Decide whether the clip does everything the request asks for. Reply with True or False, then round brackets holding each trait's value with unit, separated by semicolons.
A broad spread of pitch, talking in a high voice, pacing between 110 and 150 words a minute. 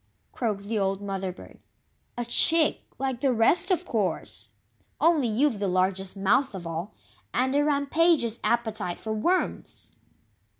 True (6.3 semitones; 230 Hz; 140 wpm)